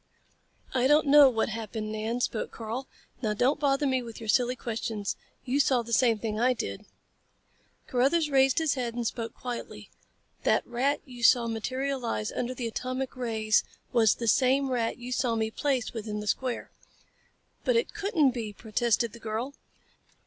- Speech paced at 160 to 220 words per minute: Yes, average, 170 wpm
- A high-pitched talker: Yes, high, 245 Hz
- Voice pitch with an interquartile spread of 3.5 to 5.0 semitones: No, average, 2.9 semitones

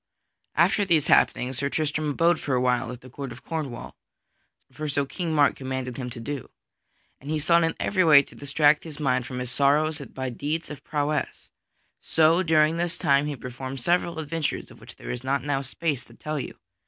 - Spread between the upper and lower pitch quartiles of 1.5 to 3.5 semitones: Yes, average, 3.1 semitones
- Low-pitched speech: No, medium, 145 Hz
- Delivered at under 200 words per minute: No, fast, 205 wpm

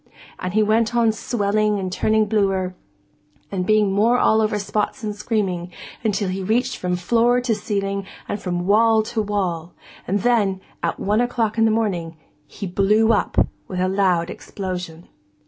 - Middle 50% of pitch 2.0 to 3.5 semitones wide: Yes, average, 2.8 semitones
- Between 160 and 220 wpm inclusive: Yes, average, 165 wpm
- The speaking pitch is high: Yes, high, 205 Hz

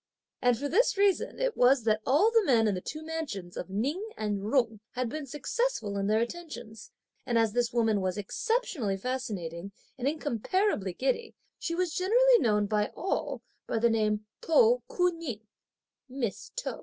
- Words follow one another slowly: No, average, 170 wpm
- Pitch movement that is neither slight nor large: No, wide, 7.9 semitones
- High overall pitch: Yes, high, 245 Hz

